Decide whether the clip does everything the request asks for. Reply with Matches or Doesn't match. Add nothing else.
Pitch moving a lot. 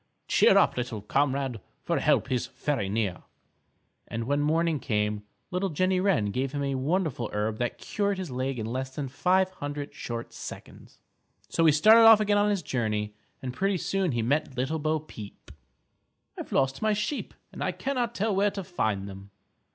Matches